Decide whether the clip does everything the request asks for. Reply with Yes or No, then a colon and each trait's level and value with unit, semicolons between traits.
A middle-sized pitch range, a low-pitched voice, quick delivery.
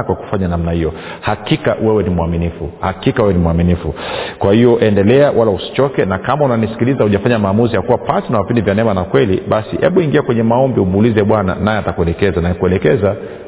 Yes: average, 4.8 semitones; low, 100 Hz; fast, 185 wpm